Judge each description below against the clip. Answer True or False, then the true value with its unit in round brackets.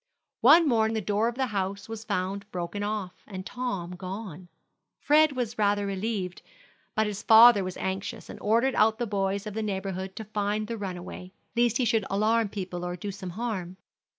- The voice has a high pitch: True (205 Hz)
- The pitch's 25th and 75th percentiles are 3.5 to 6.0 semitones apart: False (2.9 semitones)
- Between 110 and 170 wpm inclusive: False (185 wpm)